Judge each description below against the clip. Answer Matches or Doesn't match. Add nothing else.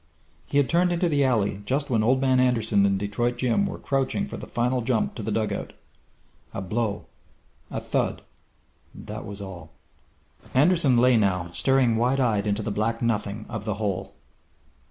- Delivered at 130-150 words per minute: Doesn't match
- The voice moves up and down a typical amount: Matches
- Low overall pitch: Matches